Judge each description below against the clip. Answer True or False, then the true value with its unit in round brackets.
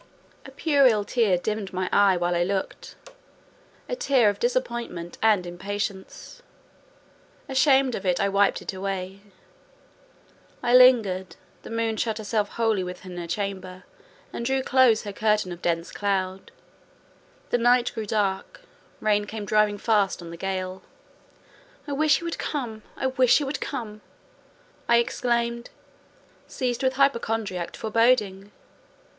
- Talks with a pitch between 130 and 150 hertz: False (215 Hz)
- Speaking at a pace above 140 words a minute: False (135 wpm)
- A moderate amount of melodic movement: True (4.4 semitones)